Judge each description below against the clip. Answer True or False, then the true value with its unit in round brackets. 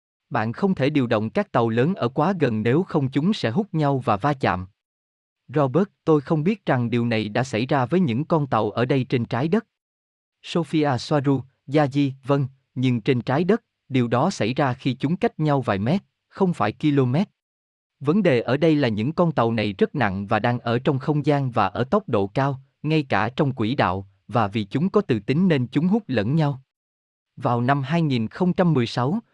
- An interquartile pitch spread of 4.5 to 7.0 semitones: True (5.1 semitones)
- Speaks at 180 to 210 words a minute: True (205 wpm)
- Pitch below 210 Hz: True (135 Hz)